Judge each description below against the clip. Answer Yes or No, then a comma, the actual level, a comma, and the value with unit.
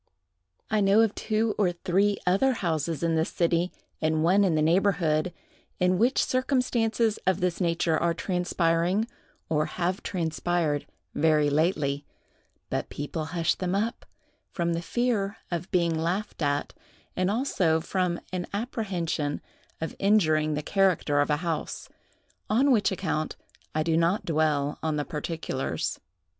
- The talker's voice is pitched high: No, medium, 175 Hz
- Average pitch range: Yes, average, 3.8 semitones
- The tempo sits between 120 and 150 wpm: Yes, average, 145 wpm